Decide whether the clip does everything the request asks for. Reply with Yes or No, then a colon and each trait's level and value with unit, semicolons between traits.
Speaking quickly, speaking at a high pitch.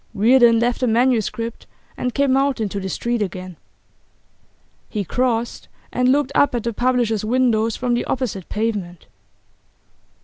No: average, 140 wpm; high, 235 Hz